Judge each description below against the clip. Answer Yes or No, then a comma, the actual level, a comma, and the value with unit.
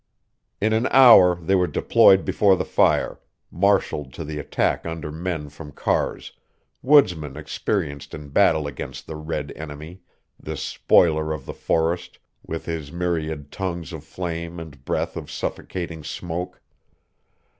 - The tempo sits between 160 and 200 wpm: No, average, 140 wpm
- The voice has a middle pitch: No, very low, 80 Hz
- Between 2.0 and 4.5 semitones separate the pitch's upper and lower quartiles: Yes, average, 2.9 semitones